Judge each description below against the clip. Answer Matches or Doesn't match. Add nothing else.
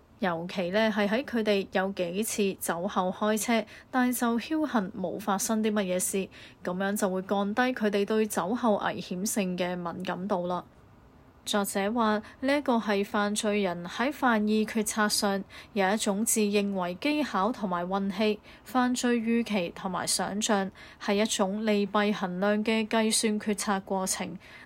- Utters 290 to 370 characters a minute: Doesn't match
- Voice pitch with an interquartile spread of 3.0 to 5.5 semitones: Doesn't match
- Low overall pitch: Doesn't match